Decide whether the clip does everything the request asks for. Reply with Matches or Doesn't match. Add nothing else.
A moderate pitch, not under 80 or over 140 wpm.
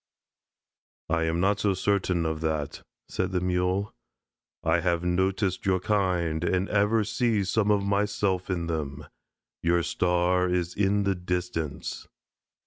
Doesn't match